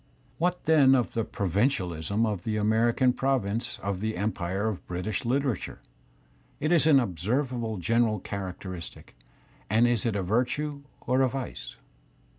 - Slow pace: No, average, 155 wpm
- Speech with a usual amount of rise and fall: Yes, average, 4.7 semitones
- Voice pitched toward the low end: Yes, low, 115 Hz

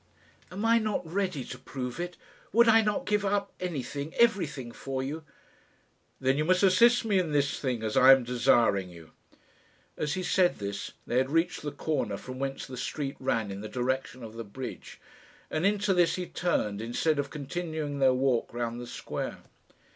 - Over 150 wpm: Yes, average, 185 wpm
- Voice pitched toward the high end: No, medium, 140 Hz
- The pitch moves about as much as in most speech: No, wide, 6.4 semitones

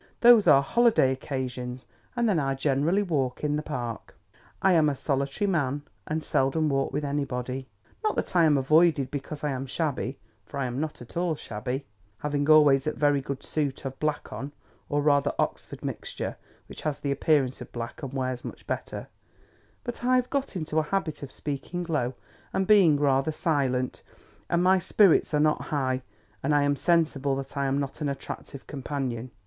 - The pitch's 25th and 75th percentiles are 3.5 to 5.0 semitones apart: No, average, 2.8 semitones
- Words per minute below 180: No, average, 185 wpm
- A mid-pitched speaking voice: Yes, medium, 145 Hz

